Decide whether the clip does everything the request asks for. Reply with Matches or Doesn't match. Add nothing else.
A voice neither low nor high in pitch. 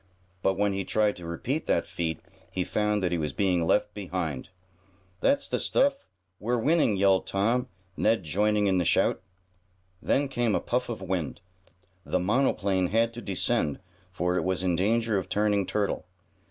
Doesn't match